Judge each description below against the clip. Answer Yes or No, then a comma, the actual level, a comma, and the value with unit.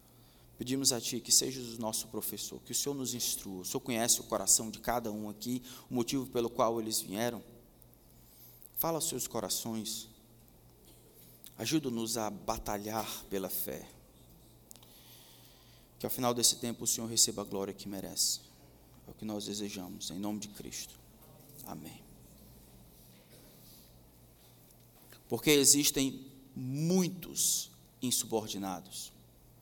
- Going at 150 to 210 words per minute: No, average, 130 wpm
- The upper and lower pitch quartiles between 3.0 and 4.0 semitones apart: Yes, average, 3.3 semitones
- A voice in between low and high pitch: No, low, 115 Hz